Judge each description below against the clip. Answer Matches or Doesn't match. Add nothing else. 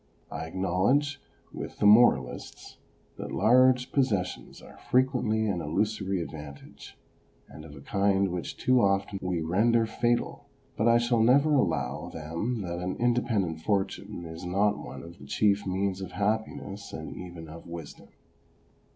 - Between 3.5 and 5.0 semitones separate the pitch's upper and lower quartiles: Doesn't match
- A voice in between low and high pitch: Doesn't match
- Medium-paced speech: Matches